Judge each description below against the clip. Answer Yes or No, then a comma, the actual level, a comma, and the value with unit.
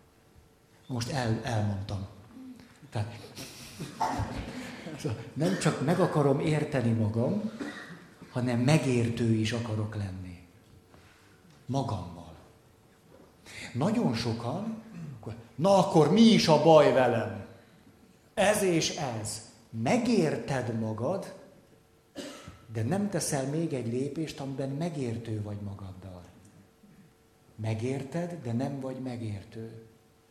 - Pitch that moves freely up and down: Yes, wide, 6.3 semitones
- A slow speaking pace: Yes, slow, 90 wpm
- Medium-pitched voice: No, low, 125 Hz